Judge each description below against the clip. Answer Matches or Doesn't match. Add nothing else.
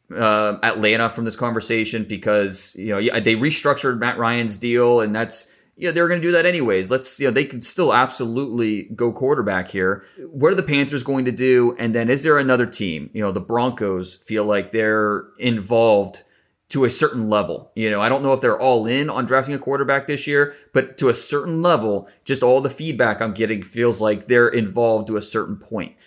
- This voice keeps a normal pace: Doesn't match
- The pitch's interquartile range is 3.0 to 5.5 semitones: Matches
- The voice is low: Matches